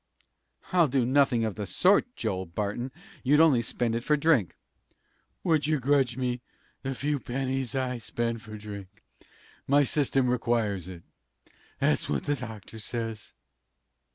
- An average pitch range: Yes, average, 4.2 semitones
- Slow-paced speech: No, average, 145 wpm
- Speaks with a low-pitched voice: Yes, low, 125 Hz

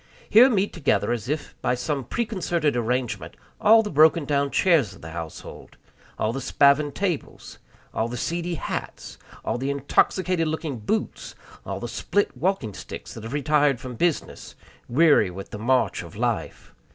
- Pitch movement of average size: No, wide, 5.9 semitones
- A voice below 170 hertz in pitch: Yes, medium, 140 Hz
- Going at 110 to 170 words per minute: Yes, average, 165 wpm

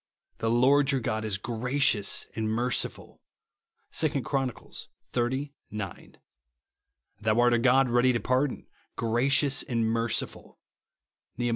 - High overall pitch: No, low, 120 Hz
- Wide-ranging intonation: No, average, 2.9 semitones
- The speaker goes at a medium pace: No, slow, 125 wpm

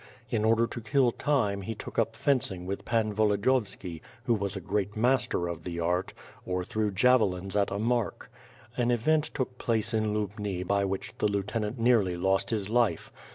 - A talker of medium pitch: No, low, 105 Hz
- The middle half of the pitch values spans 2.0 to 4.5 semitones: Yes, average, 3.4 semitones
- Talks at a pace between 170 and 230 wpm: Yes, average, 180 wpm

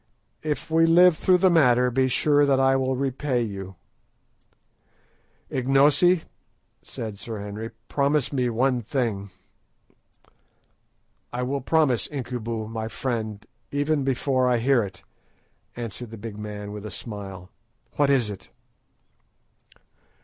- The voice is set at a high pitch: No, low, 125 Hz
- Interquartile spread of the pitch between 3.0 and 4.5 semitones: Yes, average, 4.2 semitones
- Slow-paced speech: Yes, slow, 125 wpm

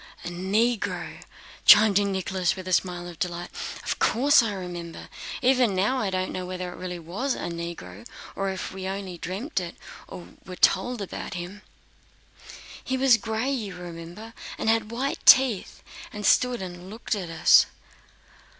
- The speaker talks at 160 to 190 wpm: Yes, average, 165 wpm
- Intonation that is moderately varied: Yes, average, 4.1 semitones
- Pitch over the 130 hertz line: Yes, high, 190 Hz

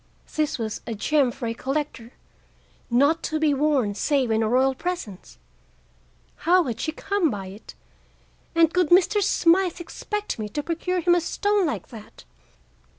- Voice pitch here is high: Yes, very high, 300 Hz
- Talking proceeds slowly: No, average, 160 wpm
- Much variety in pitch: Yes, wide, 6.7 semitones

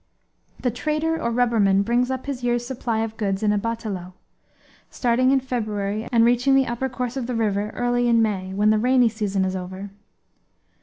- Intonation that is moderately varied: Yes, average, 3.2 semitones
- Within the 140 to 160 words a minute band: No, average, 190 wpm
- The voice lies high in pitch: Yes, high, 230 Hz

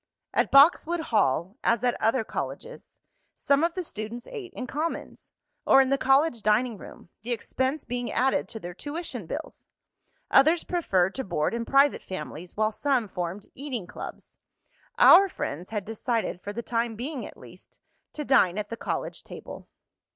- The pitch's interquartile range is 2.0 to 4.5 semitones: No, average, 5.1 semitones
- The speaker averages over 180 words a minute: No, average, 165 wpm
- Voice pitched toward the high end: Yes, high, 240 Hz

